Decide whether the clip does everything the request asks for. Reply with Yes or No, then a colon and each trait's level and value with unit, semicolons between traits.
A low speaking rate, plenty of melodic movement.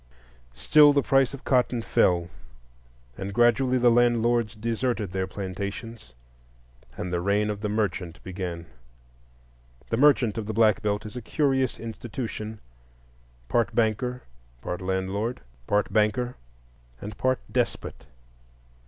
No: slow, 120 wpm; average, 4.2 semitones